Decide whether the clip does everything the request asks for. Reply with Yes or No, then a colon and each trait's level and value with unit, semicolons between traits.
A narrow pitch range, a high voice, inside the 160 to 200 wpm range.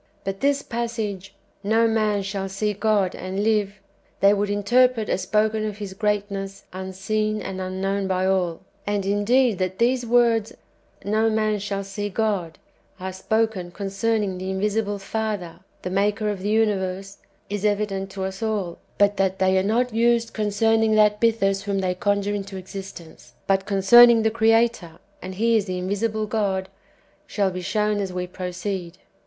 Yes: narrow, 2.3 semitones; high, 205 Hz; average, 170 wpm